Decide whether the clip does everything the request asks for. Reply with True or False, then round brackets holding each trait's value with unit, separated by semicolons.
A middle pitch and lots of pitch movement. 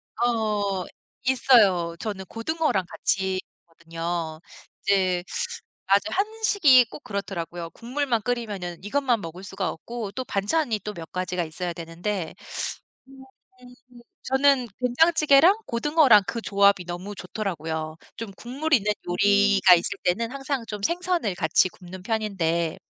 False (205 Hz; 5.7 semitones)